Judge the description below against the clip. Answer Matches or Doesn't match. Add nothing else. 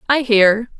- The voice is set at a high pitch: Matches